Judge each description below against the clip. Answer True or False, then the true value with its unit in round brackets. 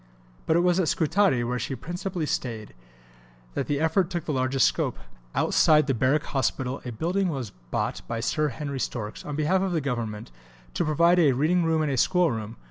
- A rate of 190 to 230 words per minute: True (200 wpm)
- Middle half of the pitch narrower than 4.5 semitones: False (5.1 semitones)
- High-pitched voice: False (150 Hz)